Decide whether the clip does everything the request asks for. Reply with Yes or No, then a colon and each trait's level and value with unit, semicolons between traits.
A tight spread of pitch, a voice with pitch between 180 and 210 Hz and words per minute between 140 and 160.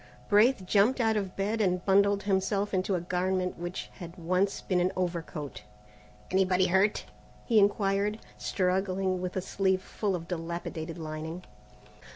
Yes: narrow, 2.0 semitones; medium, 185 Hz; average, 145 wpm